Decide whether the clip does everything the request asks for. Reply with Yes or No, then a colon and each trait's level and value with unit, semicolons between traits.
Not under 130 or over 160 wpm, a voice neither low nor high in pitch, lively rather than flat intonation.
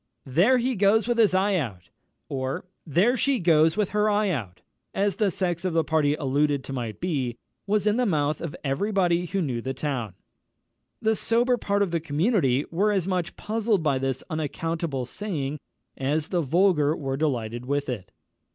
No: average, 185 wpm; medium, 165 Hz; wide, 6.7 semitones